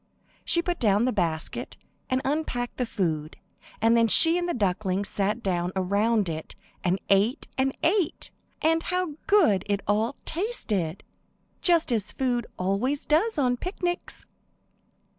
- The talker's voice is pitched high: Yes, high, 235 Hz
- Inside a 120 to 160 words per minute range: Yes, average, 140 wpm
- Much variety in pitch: Yes, wide, 8.3 semitones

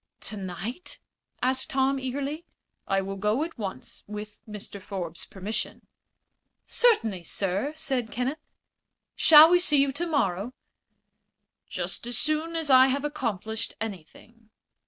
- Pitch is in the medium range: No, high, 245 Hz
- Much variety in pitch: Yes, wide, 6.5 semitones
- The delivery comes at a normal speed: No, slow, 120 wpm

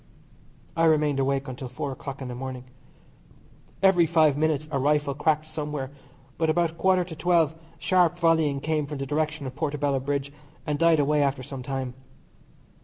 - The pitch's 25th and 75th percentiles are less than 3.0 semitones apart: Yes, narrow, 2.6 semitones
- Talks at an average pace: Yes, average, 175 wpm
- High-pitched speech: No, medium, 150 Hz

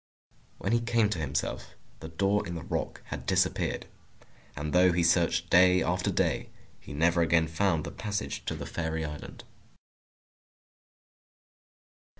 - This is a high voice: No, very low, 85 Hz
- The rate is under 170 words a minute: Yes, average, 145 wpm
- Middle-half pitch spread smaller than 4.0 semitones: Yes, narrow, 2.4 semitones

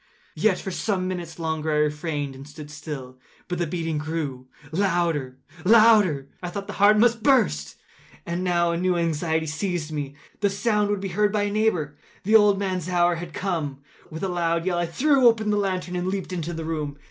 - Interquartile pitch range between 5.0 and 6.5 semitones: No, average, 4.3 semitones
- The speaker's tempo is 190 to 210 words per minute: Yes, average, 195 wpm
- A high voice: No, medium, 175 Hz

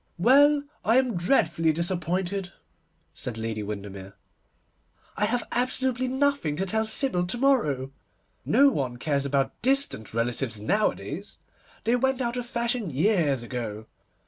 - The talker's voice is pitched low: No, medium, 180 Hz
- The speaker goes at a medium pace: No, slow, 130 wpm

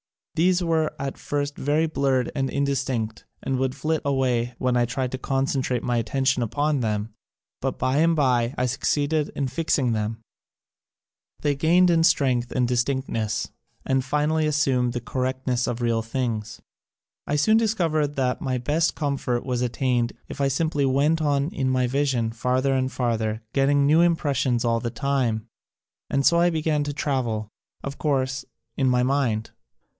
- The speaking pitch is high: No, low, 135 Hz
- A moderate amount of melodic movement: Yes, average, 3.0 semitones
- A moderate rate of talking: Yes, average, 170 wpm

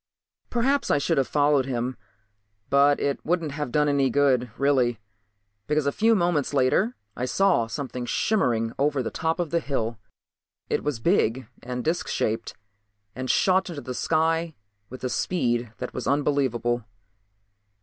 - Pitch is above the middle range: No, medium, 140 Hz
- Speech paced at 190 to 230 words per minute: No, average, 155 wpm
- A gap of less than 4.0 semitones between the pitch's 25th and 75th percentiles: No, average, 4.5 semitones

